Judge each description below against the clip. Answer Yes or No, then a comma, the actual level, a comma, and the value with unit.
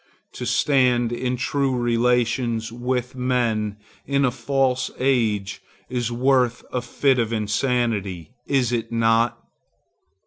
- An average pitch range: No, narrow, 2.0 semitones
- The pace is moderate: No, slow, 115 wpm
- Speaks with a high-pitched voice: No, low, 120 Hz